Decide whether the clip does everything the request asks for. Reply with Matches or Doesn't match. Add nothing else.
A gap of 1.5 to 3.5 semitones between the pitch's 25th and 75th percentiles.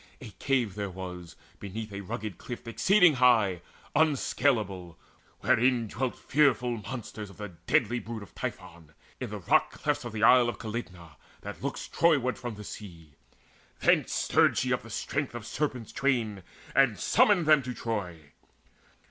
Doesn't match